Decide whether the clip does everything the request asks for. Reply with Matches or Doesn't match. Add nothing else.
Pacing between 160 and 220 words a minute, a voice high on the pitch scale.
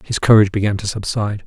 Doesn't match